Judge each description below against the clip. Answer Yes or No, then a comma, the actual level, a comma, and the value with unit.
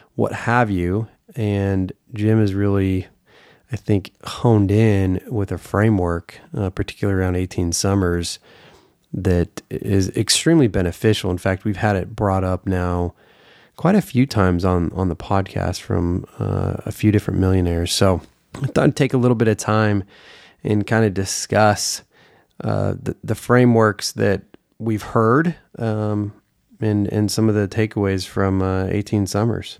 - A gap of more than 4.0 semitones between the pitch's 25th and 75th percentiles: No, average, 2.8 semitones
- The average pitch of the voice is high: No, low, 105 Hz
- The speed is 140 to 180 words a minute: Yes, average, 155 wpm